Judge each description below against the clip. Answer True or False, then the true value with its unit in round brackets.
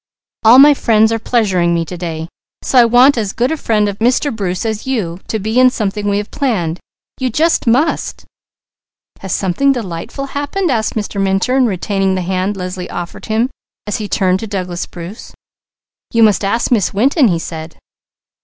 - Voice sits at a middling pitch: False (210 Hz)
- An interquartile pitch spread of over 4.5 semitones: True (4.9 semitones)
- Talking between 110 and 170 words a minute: False (180 wpm)